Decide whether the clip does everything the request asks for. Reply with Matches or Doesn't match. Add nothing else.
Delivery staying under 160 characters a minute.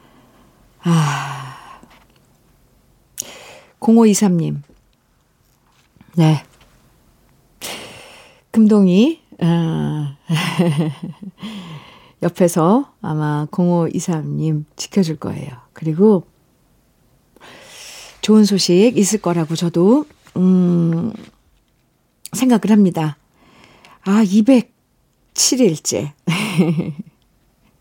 Matches